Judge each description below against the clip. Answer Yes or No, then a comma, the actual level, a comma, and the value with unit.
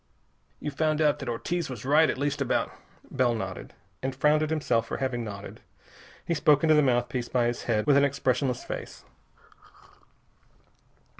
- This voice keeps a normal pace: Yes, average, 170 wpm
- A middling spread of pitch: Yes, average, 3.7 semitones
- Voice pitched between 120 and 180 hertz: Yes, low, 135 Hz